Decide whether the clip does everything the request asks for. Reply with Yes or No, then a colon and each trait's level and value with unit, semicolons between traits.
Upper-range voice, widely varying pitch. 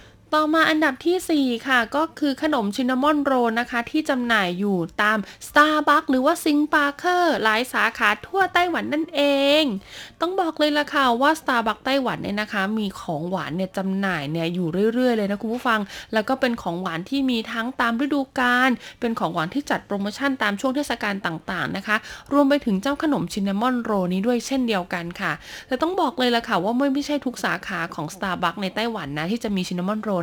Yes: high, 235 Hz; wide, 6.2 semitones